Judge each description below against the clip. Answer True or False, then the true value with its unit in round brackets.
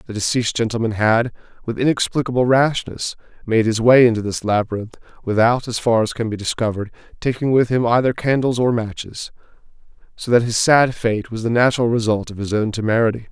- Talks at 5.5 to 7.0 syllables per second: True (5.9 syllables/s)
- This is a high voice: False (115 Hz)